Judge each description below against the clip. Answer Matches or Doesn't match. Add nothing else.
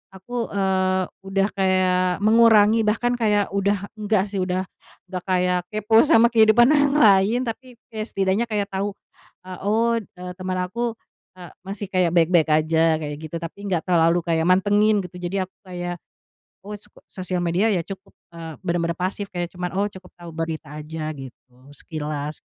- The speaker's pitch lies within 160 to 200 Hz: Matches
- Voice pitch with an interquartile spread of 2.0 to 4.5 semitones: Matches